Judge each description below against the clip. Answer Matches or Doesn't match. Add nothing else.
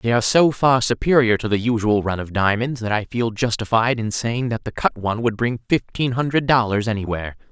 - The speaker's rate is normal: Doesn't match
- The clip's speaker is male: Matches